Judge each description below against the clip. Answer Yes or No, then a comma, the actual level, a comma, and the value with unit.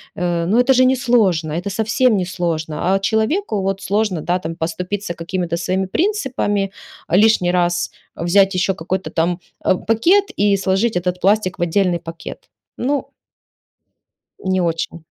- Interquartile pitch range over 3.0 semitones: Yes, average, 3.8 semitones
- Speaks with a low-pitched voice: No, high, 190 Hz